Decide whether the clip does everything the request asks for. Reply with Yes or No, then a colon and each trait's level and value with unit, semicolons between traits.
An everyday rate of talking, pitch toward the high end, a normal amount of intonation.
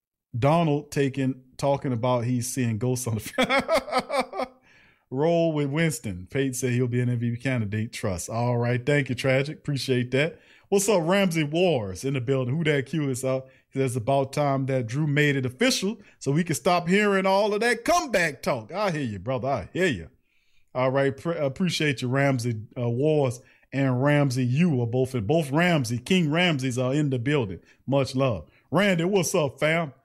No: average, 185 wpm; low, 135 Hz; average, 4.6 semitones